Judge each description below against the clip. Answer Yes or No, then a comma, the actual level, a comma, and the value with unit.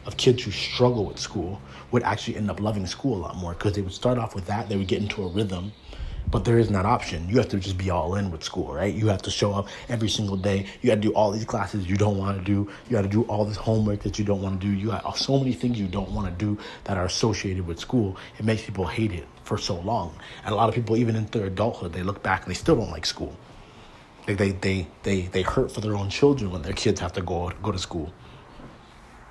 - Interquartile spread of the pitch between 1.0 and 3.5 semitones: Yes, narrow, 2.5 semitones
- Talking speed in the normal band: No, fast, 280 wpm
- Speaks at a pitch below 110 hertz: Yes, low, 100 Hz